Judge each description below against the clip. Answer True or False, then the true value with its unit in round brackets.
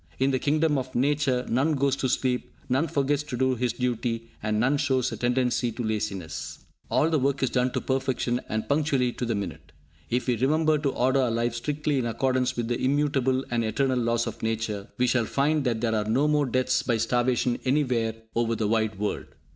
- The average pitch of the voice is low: True (125 Hz)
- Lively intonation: False (2.8 semitones)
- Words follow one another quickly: True (210 wpm)